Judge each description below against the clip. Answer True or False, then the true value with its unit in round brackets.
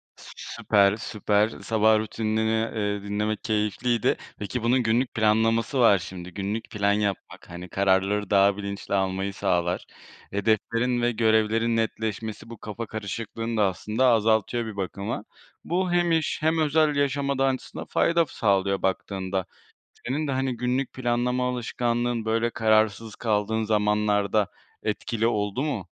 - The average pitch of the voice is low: True (110 Hz)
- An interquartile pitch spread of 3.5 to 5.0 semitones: False (2.8 semitones)